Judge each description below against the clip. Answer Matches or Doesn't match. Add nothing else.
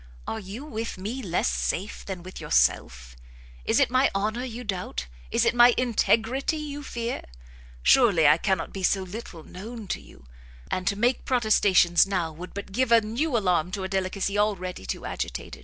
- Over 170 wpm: Matches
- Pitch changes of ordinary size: Matches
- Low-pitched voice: Doesn't match